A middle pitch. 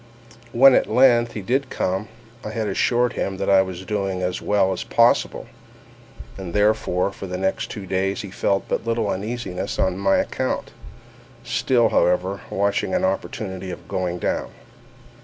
No: low, 100 Hz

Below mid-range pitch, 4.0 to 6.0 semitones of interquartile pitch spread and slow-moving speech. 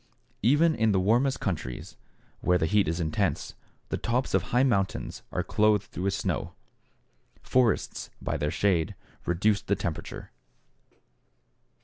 Yes: low, 100 Hz; average, 4.7 semitones; slow, 130 wpm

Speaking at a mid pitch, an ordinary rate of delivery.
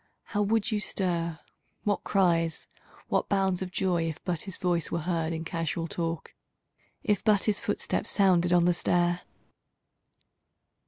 Yes: medium, 175 Hz; average, 150 wpm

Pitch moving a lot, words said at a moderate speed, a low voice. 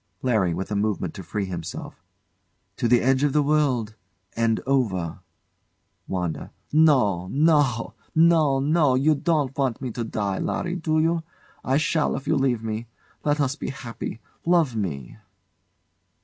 Yes: wide, 5.9 semitones; average, 150 wpm; low, 130 Hz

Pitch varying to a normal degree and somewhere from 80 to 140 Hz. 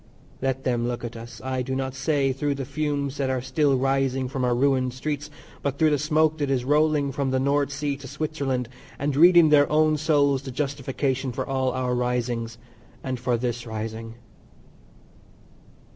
No: narrow, 2.2 semitones; low, 135 Hz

